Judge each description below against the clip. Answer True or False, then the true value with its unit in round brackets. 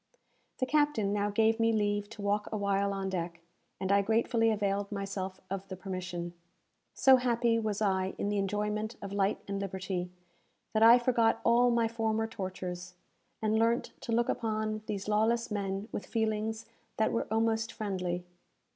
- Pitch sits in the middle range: False (210 Hz)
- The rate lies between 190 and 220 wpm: False (165 wpm)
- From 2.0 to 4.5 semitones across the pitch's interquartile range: True (2.4 semitones)